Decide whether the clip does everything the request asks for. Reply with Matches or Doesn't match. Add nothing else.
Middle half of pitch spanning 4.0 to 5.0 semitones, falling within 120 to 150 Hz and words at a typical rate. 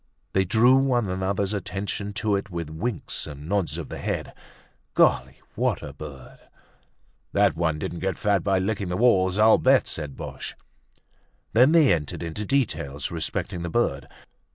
Doesn't match